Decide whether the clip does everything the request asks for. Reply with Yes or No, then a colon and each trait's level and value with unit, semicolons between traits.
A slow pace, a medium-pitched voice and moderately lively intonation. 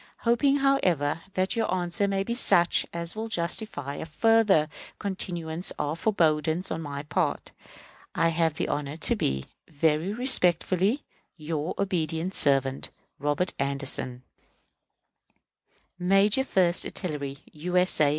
Yes: slow, 125 wpm; medium, 170 Hz; average, 4.5 semitones